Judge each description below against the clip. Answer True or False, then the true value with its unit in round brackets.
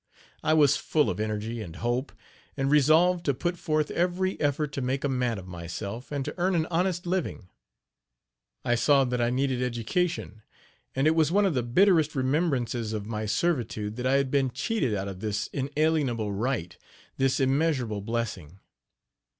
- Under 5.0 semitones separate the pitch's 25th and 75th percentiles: False (5.5 semitones)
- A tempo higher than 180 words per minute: False (175 wpm)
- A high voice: False (130 Hz)